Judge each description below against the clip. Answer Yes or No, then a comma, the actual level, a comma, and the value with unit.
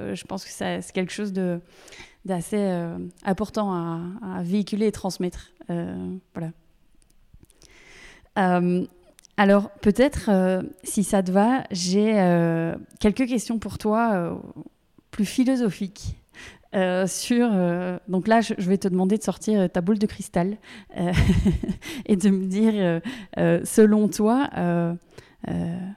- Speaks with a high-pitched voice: Yes, high, 195 Hz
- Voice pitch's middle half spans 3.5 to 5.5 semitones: No, average, 3.0 semitones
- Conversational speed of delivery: No, slow, 140 wpm